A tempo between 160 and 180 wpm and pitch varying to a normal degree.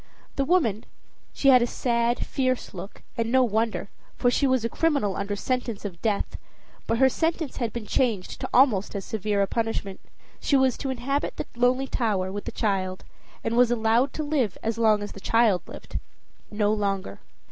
No: average, 190 wpm; average, 4.0 semitones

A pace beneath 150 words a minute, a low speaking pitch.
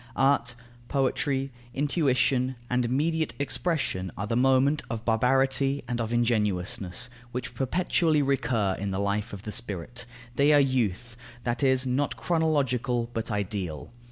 Yes: slow, 135 wpm; low, 125 Hz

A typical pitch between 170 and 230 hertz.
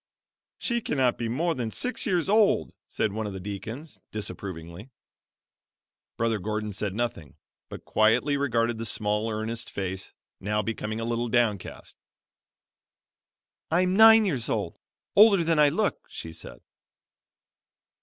No: low, 115 Hz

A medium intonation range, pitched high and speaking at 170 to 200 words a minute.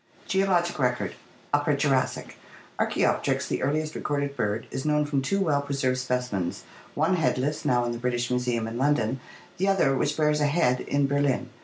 No: average, 3.3 semitones; medium, 140 Hz; average, 180 wpm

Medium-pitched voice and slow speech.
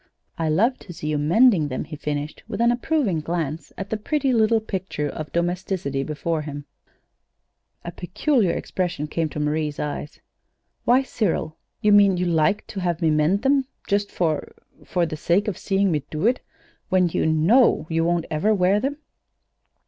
No: medium, 175 Hz; average, 175 wpm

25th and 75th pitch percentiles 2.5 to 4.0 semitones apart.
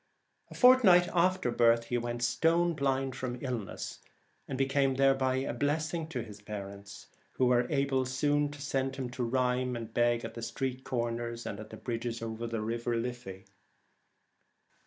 Yes: average, 2.8 semitones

